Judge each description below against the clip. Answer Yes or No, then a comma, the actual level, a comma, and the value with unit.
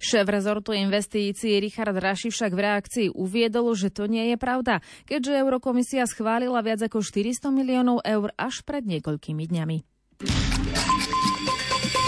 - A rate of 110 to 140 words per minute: Yes, average, 130 wpm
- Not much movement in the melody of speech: No, average, 3.6 semitones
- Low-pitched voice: No, high, 225 Hz